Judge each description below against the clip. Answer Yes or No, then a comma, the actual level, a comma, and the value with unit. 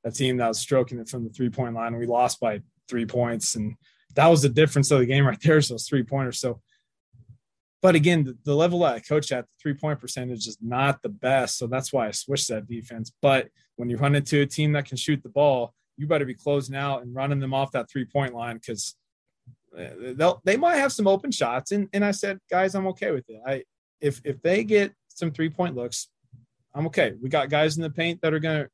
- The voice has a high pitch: No, low, 135 Hz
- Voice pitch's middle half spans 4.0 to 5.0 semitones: Yes, average, 4.3 semitones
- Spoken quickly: Yes, fast, 235 wpm